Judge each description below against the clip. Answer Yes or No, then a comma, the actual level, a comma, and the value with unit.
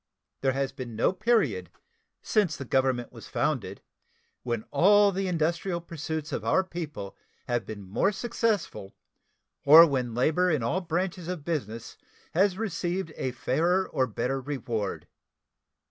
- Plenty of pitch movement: Yes, wide, 6.4 semitones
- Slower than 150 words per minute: Yes, average, 140 wpm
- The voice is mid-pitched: Yes, medium, 155 Hz